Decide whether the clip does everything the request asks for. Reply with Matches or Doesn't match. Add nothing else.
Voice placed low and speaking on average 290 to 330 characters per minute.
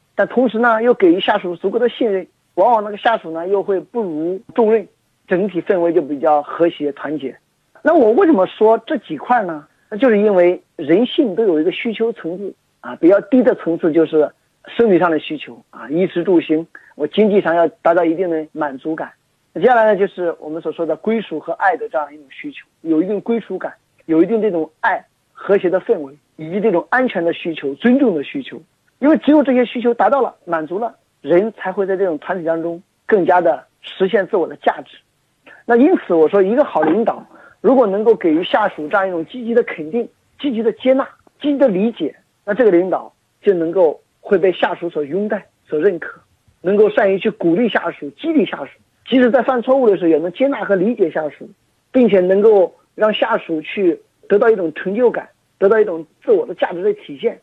Doesn't match